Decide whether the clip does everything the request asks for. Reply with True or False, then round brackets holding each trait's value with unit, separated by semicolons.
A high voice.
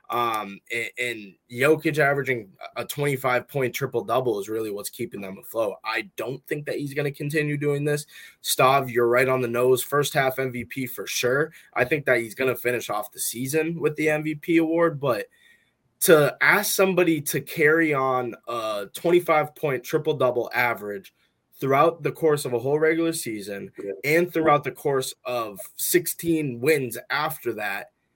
False (140 Hz)